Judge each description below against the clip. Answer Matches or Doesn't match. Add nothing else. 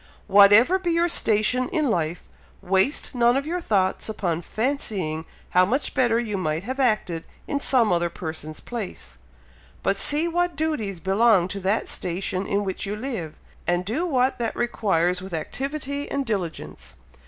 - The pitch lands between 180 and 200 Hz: Doesn't match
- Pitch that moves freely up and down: Matches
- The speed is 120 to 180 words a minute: Matches